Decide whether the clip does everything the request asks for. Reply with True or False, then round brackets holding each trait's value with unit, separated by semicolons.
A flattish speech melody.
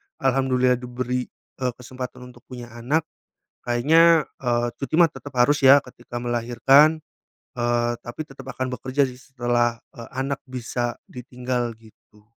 True (1.9 semitones)